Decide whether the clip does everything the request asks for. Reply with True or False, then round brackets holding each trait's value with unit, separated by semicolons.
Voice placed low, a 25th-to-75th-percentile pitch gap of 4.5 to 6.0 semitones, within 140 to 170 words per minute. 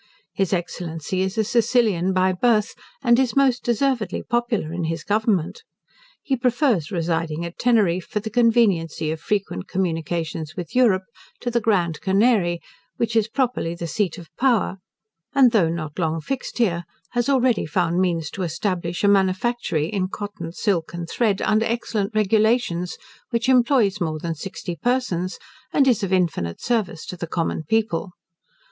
False (195 Hz; 5.5 semitones; 160 wpm)